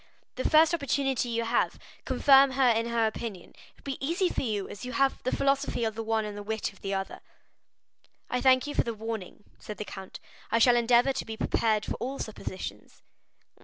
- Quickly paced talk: Yes, fast, 210 wpm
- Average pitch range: Yes, average, 3.7 semitones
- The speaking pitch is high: Yes, high, 235 Hz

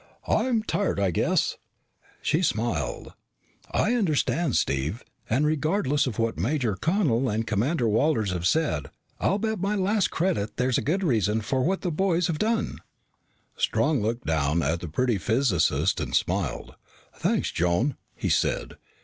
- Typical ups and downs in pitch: No, wide, 8.7 semitones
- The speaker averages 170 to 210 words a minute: No, average, 150 wpm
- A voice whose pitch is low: Yes, low, 130 Hz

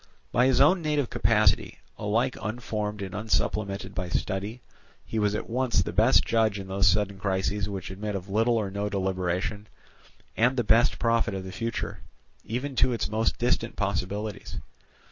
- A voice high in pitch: No, low, 105 Hz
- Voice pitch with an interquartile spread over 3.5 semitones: No, average, 3.0 semitones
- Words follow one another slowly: No, average, 170 wpm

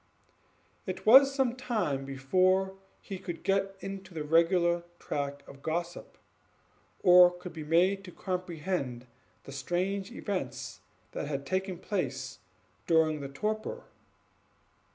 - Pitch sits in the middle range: Yes, medium, 180 Hz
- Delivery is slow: Yes, slow, 120 wpm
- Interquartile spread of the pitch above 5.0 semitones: No, average, 4.2 semitones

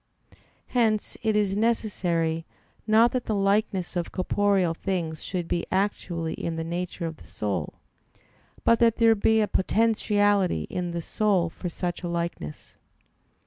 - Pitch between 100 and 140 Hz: No, high, 190 Hz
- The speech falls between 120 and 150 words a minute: Yes, average, 145 wpm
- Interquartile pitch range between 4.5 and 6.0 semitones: No, average, 3.9 semitones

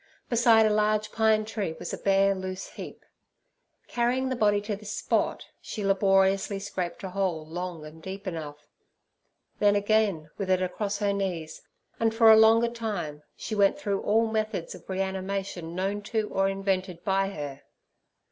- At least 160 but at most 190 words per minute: Yes, average, 165 wpm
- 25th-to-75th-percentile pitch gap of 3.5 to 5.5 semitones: No, narrow, 2.5 semitones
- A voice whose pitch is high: Yes, high, 195 Hz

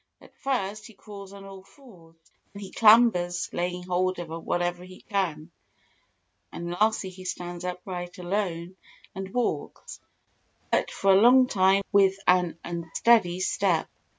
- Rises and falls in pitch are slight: Yes, narrow, 2.3 semitones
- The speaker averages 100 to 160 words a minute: Yes, average, 140 wpm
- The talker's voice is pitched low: No, medium, 185 Hz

